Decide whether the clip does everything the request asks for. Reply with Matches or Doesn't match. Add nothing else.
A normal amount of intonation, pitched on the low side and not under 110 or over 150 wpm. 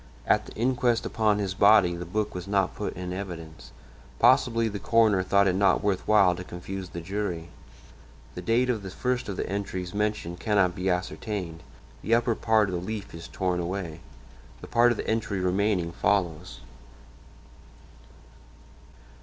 Doesn't match